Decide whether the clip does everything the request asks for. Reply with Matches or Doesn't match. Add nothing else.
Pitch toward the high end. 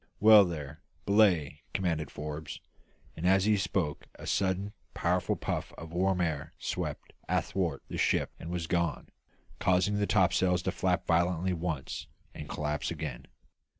Doesn't match